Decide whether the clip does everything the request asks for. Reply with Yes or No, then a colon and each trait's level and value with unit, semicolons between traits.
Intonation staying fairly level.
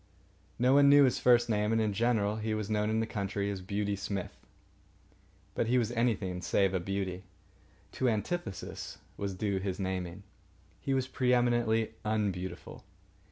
No: average, 3.5 semitones